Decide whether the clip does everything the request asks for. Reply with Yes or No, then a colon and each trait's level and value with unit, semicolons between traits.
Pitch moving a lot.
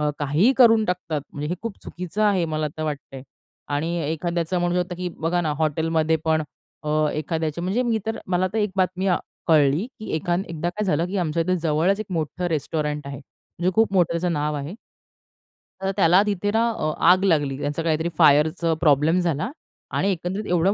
No: average, 3.3 semitones